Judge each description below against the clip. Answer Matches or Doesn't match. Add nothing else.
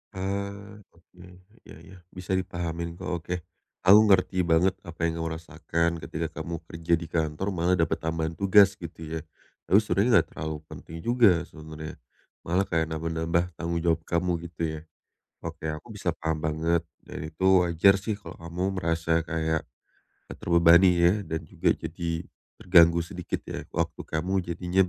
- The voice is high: Doesn't match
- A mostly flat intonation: Matches